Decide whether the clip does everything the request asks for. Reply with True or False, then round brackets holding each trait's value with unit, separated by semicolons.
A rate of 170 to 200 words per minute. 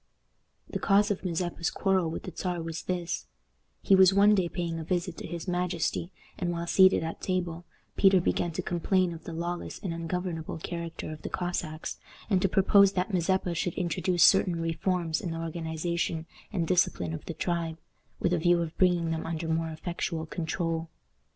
True (185 wpm)